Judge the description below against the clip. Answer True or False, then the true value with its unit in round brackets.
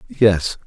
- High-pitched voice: False (90 Hz)